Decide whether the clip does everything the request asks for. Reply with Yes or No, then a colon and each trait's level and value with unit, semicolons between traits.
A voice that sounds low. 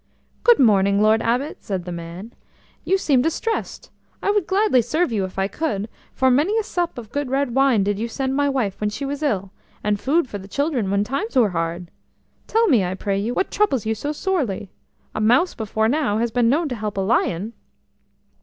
No: high, 235 Hz